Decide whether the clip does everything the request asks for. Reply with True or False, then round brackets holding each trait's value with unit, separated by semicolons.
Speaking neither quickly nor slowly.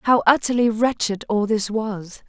True (160 wpm)